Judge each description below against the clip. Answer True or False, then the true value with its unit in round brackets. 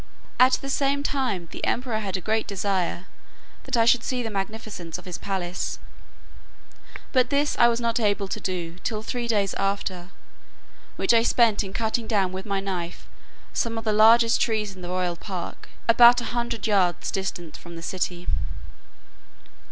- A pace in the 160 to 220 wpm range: True (175 wpm)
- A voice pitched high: True (210 Hz)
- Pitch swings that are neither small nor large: True (4.1 semitones)